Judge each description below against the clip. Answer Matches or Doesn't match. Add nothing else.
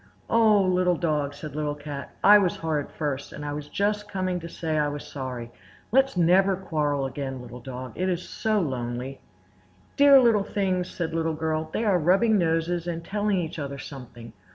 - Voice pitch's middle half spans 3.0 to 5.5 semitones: Matches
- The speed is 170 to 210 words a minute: Matches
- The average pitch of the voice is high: Doesn't match